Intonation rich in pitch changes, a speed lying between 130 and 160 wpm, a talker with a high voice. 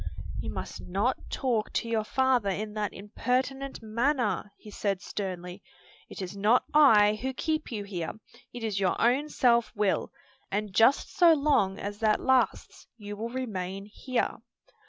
No: average, 4.0 semitones; average, 155 wpm; high, 215 Hz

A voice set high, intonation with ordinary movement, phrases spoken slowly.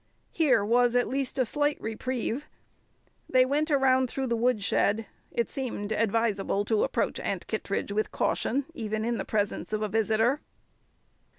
No: high, 235 Hz; average, 3.2 semitones; average, 155 wpm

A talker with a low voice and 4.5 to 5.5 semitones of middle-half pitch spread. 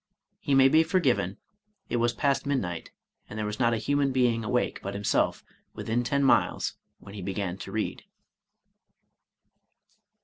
Yes: low, 120 Hz; average, 4.9 semitones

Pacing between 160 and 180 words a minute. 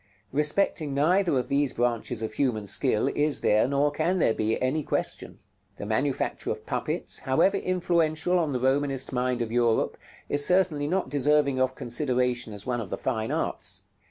Yes: average, 170 wpm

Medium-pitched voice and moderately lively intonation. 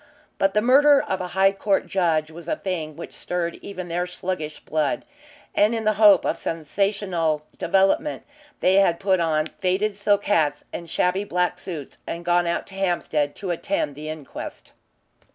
Yes: medium, 180 Hz; average, 3.3 semitones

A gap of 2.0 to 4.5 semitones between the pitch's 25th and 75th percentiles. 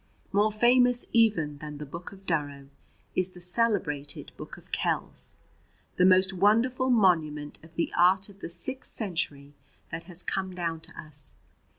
No: average, 5.1 semitones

